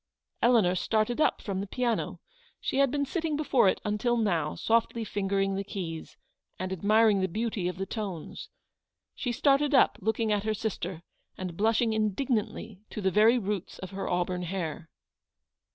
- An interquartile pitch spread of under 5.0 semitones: Yes, average, 3.6 semitones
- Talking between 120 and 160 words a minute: No, average, 170 wpm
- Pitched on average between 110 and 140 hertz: No, high, 210 Hz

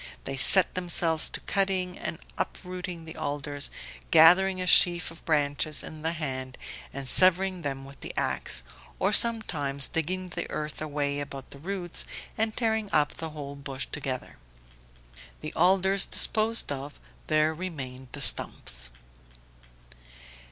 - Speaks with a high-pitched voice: No, medium, 160 Hz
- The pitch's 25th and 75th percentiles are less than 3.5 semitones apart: No, average, 4.5 semitones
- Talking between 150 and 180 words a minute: No, slow, 135 wpm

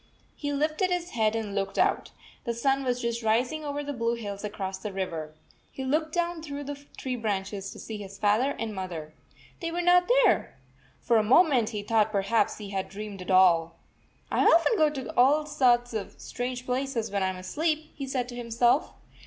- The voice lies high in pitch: Yes, high, 235 Hz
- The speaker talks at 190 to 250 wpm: Yes, average, 200 wpm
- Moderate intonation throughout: No, wide, 6.0 semitones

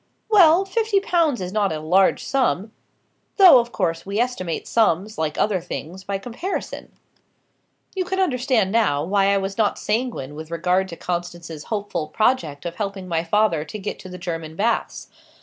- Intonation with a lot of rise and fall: Yes, wide, 5.9 semitones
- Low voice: No, high, 195 Hz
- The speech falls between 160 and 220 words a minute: Yes, average, 170 wpm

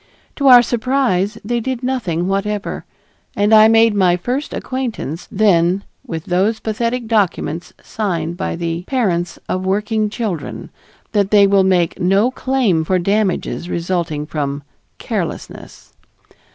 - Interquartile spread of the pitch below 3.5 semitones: No, average, 4.5 semitones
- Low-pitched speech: No, high, 200 Hz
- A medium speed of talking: No, slow, 130 wpm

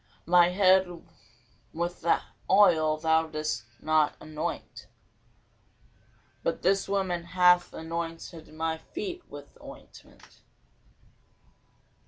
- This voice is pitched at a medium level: Yes, medium, 170 Hz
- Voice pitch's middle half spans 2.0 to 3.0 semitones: Yes, narrow, 2.6 semitones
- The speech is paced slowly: Yes, slow, 85 wpm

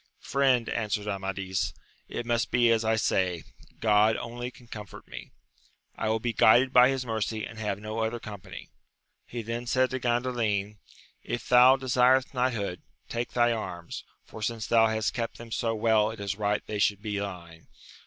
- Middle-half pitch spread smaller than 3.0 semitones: Yes, narrow, 2.6 semitones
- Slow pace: No, average, 175 wpm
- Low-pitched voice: Yes, low, 110 Hz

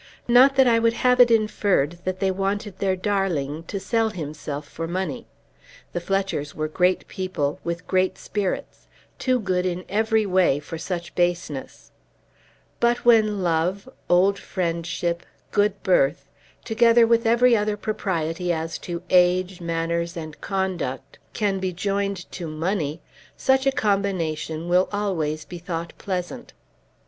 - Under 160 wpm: Yes, average, 140 wpm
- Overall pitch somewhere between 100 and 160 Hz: No, medium, 185 Hz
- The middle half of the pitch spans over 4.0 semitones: No, average, 3.7 semitones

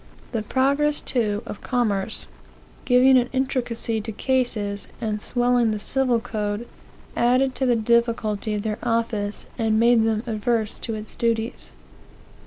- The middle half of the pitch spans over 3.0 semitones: No, narrow, 2.4 semitones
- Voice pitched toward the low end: No, high, 230 Hz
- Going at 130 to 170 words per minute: Yes, average, 140 wpm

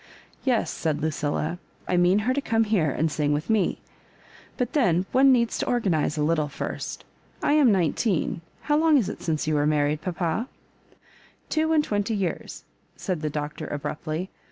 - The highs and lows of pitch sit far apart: Yes, wide, 7.2 semitones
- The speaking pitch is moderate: Yes, medium, 175 Hz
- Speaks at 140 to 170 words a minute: No, average, 190 wpm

